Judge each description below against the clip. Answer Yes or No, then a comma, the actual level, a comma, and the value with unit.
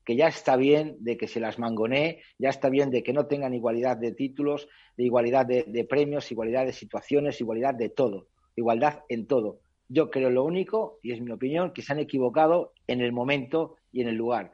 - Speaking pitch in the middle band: No, low, 130 Hz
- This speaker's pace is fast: Yes, fast, 215 wpm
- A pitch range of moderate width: Yes, average, 3.5 semitones